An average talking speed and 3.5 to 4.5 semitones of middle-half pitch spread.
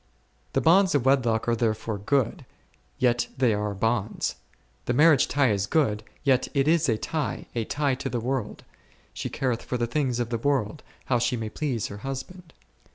Yes: average, 185 wpm; average, 3.9 semitones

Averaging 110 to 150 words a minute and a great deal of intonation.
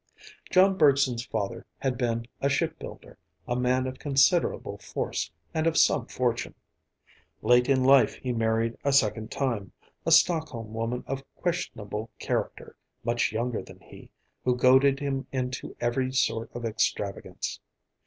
No: average, 140 wpm; average, 2.9 semitones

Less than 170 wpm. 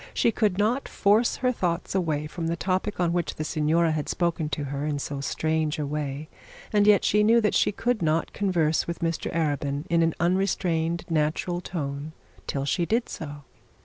No: average, 190 wpm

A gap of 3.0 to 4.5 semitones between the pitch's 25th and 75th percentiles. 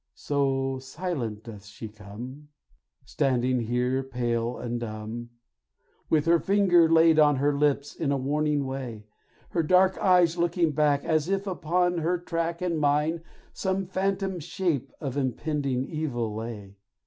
No: average, 5.3 semitones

